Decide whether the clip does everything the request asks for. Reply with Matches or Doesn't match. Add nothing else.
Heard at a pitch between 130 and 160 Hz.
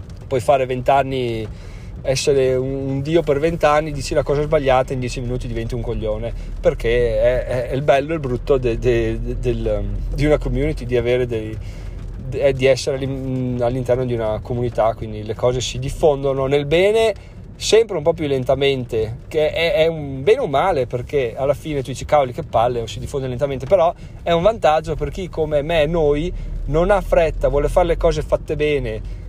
Matches